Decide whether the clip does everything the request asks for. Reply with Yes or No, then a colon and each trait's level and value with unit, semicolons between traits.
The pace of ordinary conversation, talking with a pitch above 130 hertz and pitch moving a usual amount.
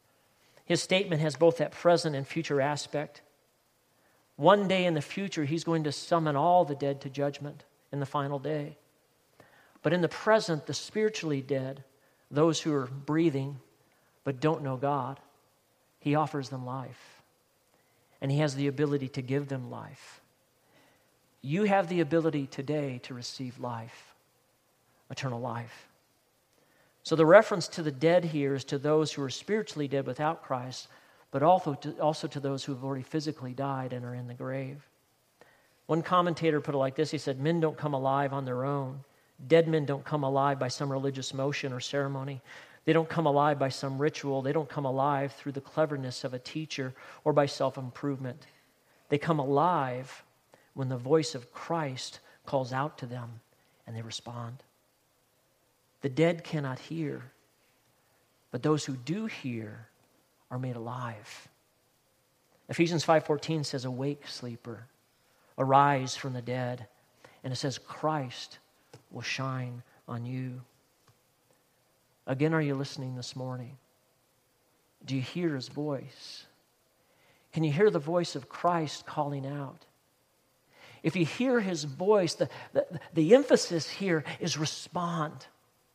Yes: average, 155 wpm; medium, 140 Hz; average, 3.3 semitones